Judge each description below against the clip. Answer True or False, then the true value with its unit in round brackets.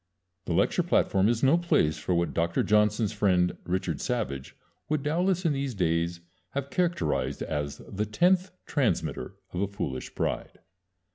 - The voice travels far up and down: True (8.7 semitones)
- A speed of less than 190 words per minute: True (150 wpm)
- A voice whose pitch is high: False (105 Hz)